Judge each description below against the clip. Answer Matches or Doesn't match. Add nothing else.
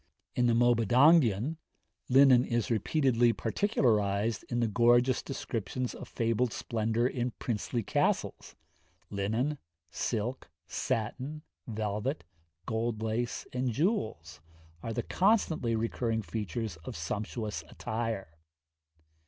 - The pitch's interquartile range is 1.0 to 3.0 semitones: Matches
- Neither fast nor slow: Doesn't match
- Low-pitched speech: Matches